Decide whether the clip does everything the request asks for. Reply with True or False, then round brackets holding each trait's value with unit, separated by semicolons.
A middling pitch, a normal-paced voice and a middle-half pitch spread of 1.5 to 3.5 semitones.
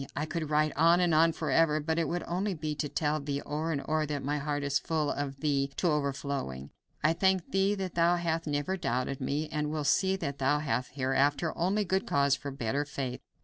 False (150 Hz; 220 wpm; 2.9 semitones)